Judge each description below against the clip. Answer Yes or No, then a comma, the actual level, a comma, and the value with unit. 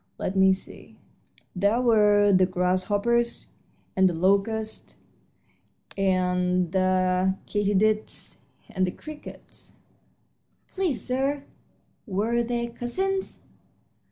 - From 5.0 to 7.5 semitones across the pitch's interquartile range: No, average, 4.2 semitones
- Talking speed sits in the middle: No, slow, 90 wpm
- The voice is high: Yes, high, 205 Hz